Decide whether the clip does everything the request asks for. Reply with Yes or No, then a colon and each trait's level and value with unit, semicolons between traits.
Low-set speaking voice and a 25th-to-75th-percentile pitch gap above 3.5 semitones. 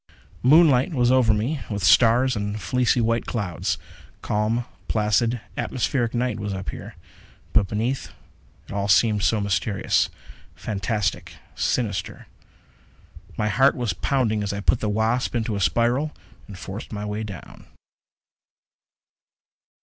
No: low, 110 Hz; average, 3.1 semitones